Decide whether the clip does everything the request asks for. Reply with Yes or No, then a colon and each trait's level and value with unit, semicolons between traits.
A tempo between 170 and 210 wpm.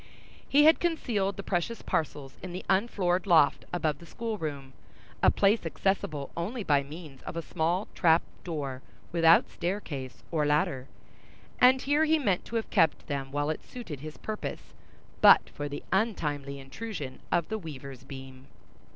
No: average, 160 wpm